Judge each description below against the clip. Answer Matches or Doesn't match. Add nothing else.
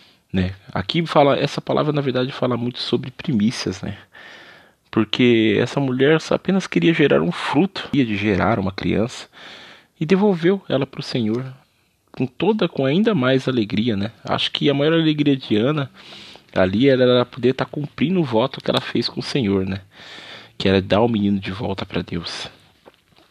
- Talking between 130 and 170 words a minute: Doesn't match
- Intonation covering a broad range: Matches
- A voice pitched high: Doesn't match